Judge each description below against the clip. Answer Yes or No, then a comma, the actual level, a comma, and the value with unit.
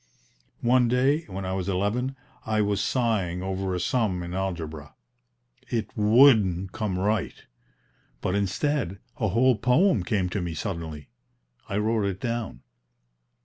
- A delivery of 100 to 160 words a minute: Yes, average, 140 wpm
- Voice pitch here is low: Yes, low, 100 Hz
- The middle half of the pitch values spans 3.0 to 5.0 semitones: Yes, average, 4.3 semitones